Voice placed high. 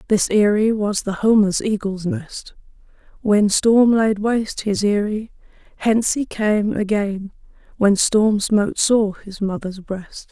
Yes: high, 210 Hz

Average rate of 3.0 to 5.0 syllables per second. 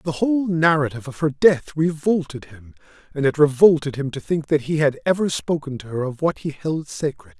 No: 5.5 syllables/s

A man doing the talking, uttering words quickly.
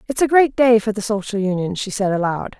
No: female; fast, 255 wpm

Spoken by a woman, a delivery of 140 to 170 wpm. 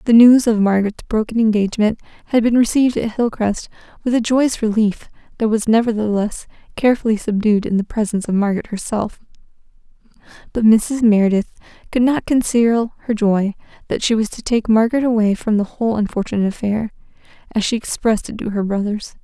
Yes: female; average, 165 wpm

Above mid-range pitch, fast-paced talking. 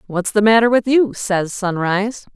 No: high, 210 Hz; average, 180 wpm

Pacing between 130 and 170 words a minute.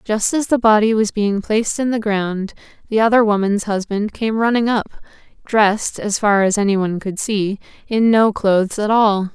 No: average, 185 wpm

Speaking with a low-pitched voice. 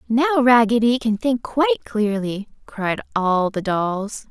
No: high, 230 Hz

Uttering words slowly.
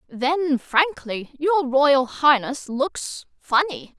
Yes: slow, 90 wpm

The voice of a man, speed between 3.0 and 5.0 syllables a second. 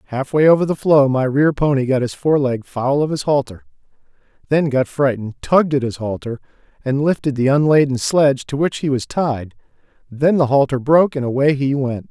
No: male; 5.6 syllables/s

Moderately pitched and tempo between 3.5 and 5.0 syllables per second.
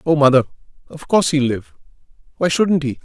No: medium, 150 Hz; 6.0 syllables/s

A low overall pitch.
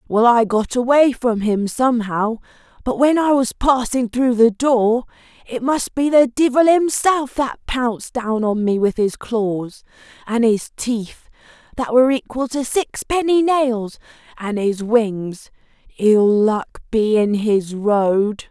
No: high, 235 Hz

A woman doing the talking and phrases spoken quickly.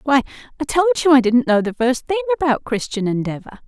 Yes: female; fast, 215 wpm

